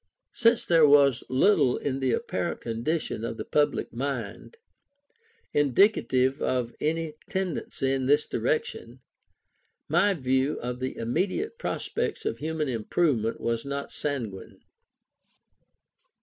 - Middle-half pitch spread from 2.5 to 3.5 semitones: No, average, 4.7 semitones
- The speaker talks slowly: Yes, slow, 115 wpm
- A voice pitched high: No, medium, 140 Hz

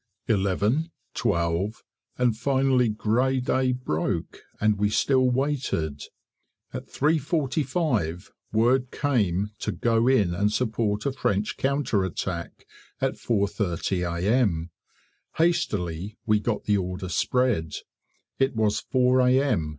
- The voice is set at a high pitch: No, low, 110 Hz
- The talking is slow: Yes, slow, 110 wpm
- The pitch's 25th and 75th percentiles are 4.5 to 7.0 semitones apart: Yes, wide, 5.4 semitones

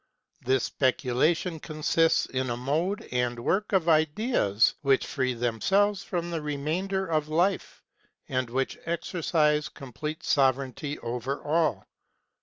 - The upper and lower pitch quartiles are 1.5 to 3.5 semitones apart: No, average, 4.7 semitones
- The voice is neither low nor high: Yes, medium, 150 Hz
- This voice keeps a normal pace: No, slow, 130 wpm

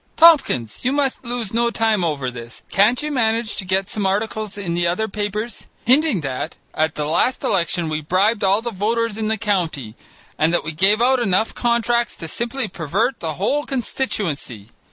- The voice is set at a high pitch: Yes, high, 210 Hz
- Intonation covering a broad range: Yes, wide, 5.7 semitones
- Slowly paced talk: No, average, 185 wpm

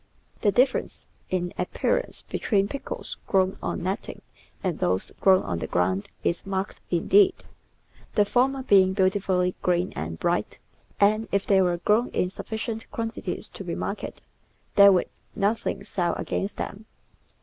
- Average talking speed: Yes, average, 150 wpm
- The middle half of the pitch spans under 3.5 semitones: Yes, average, 3.0 semitones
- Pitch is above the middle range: Yes, high, 195 Hz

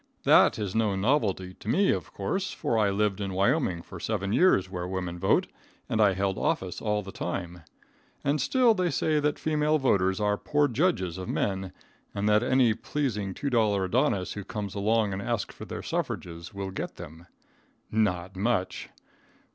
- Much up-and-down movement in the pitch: No, average, 4.9 semitones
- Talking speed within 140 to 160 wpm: No, average, 175 wpm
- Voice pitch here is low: Yes, low, 105 Hz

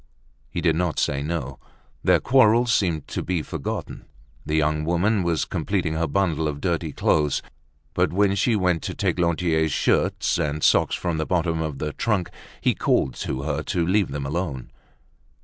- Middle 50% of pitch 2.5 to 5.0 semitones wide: Yes, average, 3.2 semitones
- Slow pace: No, average, 175 wpm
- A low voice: Yes, very low, 80 Hz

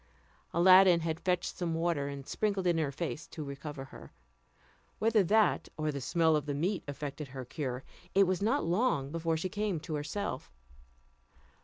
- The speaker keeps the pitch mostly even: No, average, 4.5 semitones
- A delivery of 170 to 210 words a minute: Yes, average, 175 wpm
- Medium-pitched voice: Yes, medium, 165 Hz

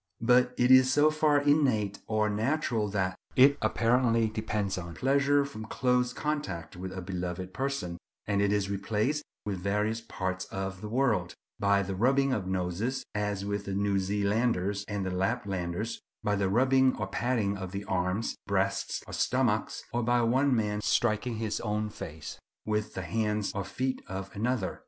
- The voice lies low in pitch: Yes, low, 105 Hz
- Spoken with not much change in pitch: No, average, 4.3 semitones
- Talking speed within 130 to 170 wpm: Yes, average, 165 wpm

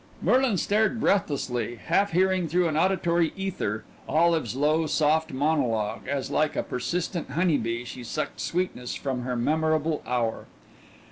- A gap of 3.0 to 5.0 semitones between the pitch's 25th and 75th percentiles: No, wide, 5.6 semitones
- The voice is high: No, medium, 155 Hz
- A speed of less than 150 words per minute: Yes, average, 140 wpm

